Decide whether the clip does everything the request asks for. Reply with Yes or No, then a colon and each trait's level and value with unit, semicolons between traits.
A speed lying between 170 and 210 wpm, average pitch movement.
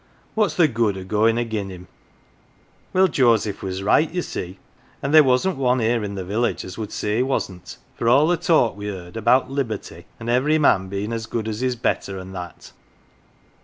Yes: average, 200 wpm; average, 4.8 semitones